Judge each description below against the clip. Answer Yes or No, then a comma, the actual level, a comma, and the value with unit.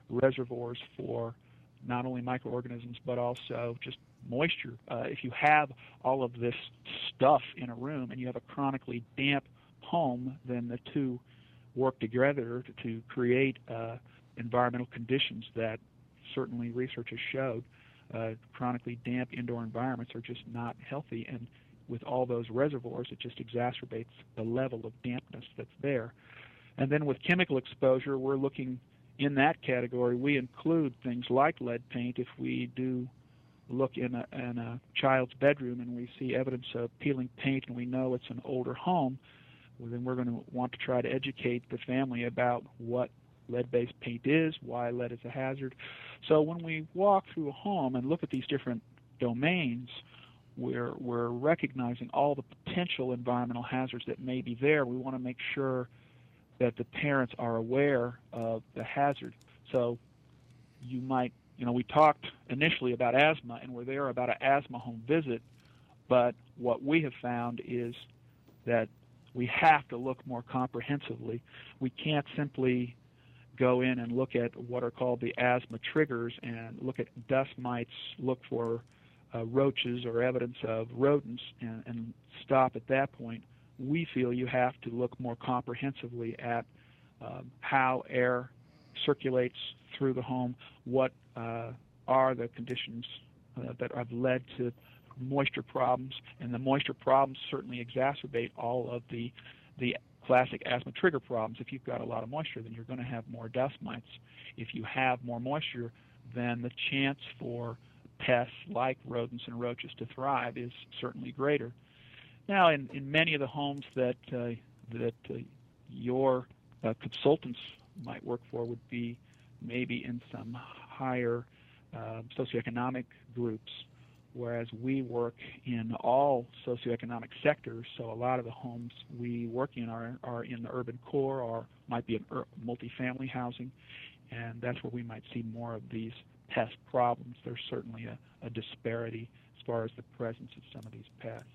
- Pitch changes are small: Yes, narrow, 1.8 semitones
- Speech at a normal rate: Yes, average, 165 wpm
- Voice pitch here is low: Yes, low, 125 Hz